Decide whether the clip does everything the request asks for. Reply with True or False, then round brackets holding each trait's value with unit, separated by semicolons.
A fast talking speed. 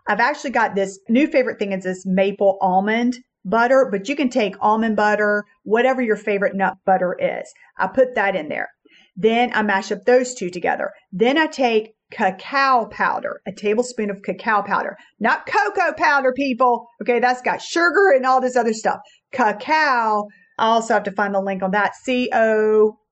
False (185 wpm)